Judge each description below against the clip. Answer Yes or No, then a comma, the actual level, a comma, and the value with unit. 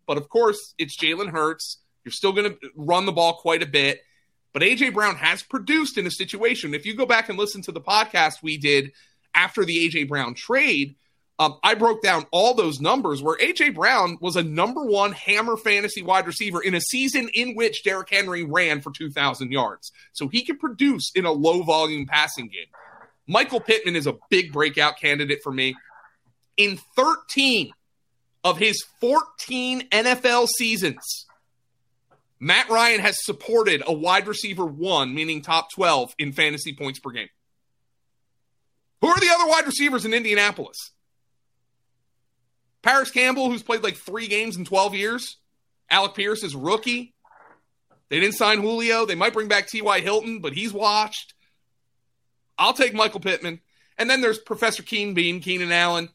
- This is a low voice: No, high, 195 Hz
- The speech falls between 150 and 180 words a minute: Yes, average, 170 wpm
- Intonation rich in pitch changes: Yes, wide, 7.3 semitones